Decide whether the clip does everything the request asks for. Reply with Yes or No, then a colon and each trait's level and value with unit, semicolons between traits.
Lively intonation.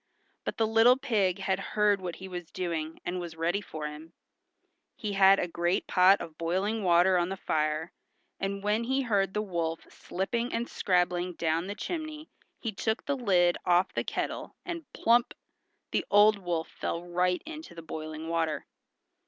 No: average, 3.8 semitones